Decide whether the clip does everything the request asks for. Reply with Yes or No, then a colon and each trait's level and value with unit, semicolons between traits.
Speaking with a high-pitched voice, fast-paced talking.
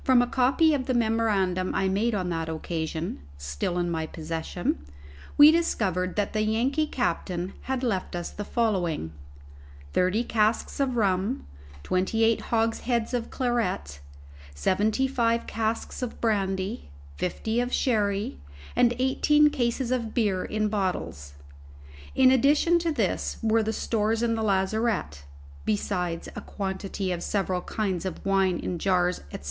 No: high, 210 Hz; average, 145 wpm